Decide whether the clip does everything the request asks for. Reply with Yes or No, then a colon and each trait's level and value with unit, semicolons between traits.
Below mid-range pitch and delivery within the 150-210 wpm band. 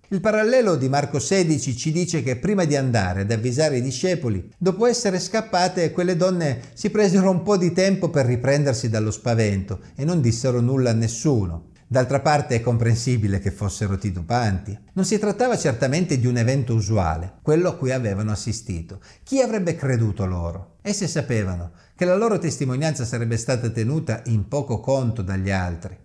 Yes: low, 130 Hz; fast, 170 wpm